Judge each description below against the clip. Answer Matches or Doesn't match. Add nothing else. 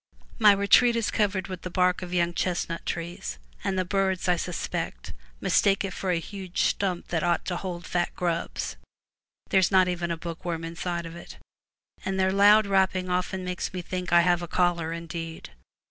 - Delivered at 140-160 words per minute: Doesn't match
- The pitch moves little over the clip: Matches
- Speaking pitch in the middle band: Matches